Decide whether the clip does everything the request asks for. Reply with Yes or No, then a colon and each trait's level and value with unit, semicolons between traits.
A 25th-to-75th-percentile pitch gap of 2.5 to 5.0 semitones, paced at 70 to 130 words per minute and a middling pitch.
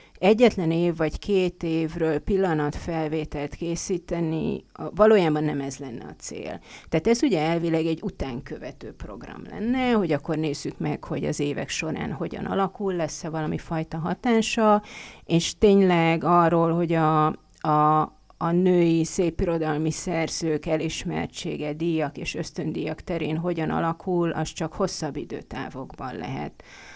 Yes: average, 2.8 semitones; average, 125 wpm; medium, 165 Hz